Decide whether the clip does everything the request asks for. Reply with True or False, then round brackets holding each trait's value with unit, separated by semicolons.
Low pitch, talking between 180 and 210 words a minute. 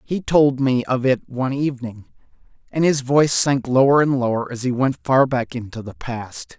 True (130 Hz; 200 wpm)